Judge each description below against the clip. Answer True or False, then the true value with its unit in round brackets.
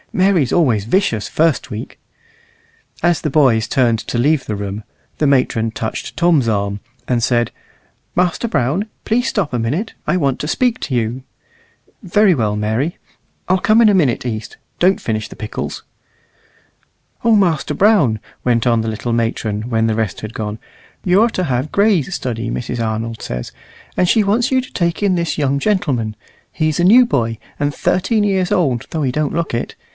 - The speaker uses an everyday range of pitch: False (8.1 semitones)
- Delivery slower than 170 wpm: False (180 wpm)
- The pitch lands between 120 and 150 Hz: True (140 Hz)